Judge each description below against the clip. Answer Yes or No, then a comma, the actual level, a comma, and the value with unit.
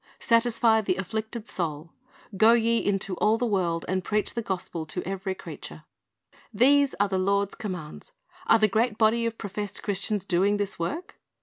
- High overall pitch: Yes, high, 205 Hz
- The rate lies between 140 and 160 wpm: No, average, 170 wpm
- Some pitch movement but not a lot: Yes, average, 3.2 semitones